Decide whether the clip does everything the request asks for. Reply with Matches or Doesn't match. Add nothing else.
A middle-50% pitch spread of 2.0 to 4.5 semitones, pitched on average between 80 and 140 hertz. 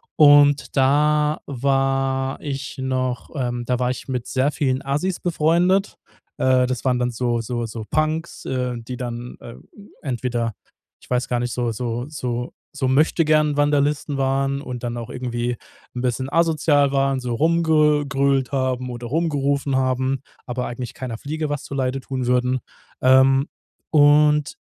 Matches